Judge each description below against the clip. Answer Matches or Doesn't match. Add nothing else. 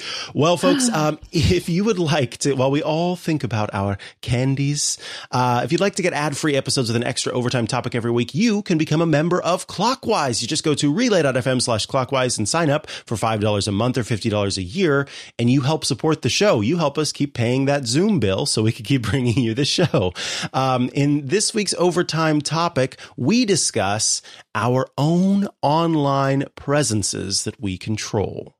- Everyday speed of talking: Matches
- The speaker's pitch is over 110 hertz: Matches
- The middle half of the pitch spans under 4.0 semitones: Doesn't match